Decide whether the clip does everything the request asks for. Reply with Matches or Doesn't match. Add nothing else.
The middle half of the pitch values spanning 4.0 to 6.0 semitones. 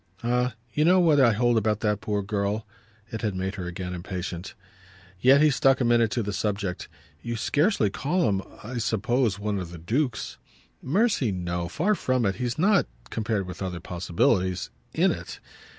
Matches